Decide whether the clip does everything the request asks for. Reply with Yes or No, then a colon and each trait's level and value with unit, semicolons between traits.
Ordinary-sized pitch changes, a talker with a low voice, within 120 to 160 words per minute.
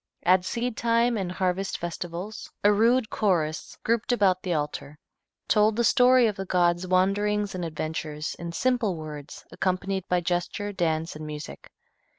No: average, 3.9 semitones; medium, 185 Hz; average, 155 wpm